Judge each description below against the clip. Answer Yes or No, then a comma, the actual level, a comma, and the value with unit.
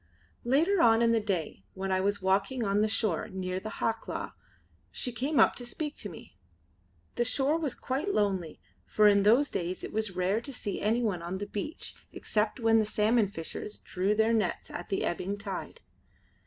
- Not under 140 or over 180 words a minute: No, average, 190 wpm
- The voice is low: No, high, 210 Hz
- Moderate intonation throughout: Yes, average, 3.7 semitones